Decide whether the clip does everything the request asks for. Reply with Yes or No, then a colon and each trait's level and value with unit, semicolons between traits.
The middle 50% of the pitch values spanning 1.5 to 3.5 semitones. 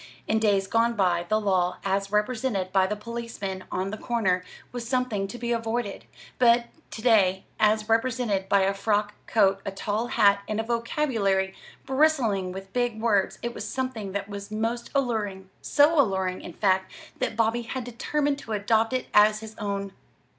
Yes: average, 3.2 semitones